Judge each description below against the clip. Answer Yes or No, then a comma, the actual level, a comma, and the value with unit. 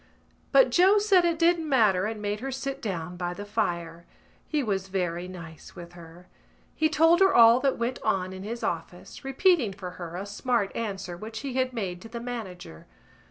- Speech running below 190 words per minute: No, average, 195 wpm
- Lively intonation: Yes, wide, 6.8 semitones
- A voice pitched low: No, high, 210 Hz